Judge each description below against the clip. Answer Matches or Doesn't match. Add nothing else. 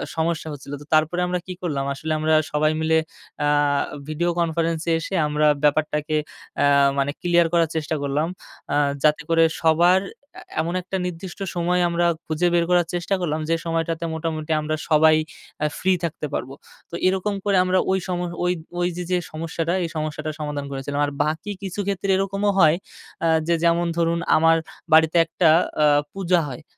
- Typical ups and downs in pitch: Doesn't match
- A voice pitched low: Doesn't match